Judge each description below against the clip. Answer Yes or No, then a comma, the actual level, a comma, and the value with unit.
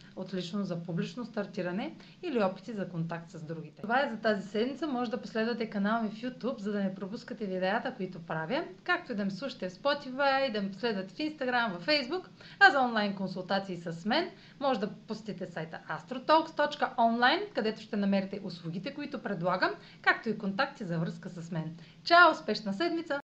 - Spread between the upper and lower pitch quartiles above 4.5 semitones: Yes, wide, 5.4 semitones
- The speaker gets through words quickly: Yes, fast, 180 wpm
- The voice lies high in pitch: Yes, high, 215 Hz